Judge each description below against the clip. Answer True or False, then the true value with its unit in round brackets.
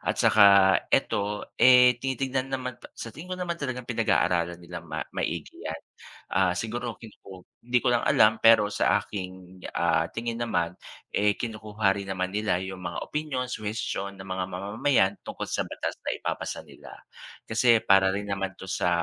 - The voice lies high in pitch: False (105 Hz)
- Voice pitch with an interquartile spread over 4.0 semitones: True (4.4 semitones)